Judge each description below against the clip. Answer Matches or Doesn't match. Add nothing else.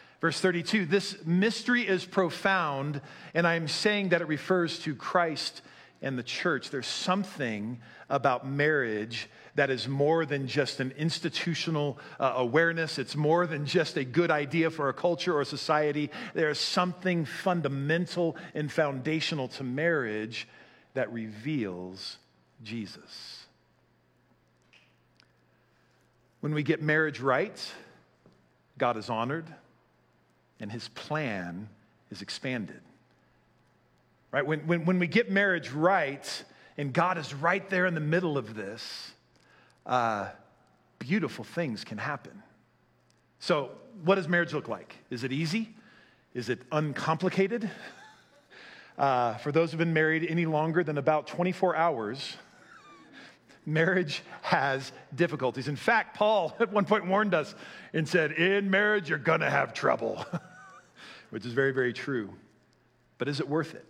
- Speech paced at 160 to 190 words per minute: Doesn't match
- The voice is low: Doesn't match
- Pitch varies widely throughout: Doesn't match